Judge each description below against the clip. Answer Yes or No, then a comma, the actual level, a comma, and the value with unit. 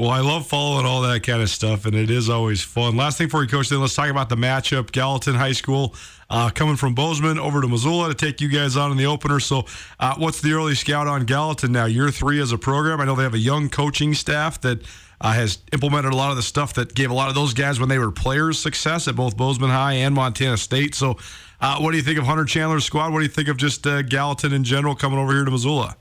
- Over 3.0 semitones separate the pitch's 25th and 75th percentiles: No, narrow, 2.5 semitones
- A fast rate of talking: Yes, fast, 270 wpm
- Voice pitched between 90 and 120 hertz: No, low, 135 Hz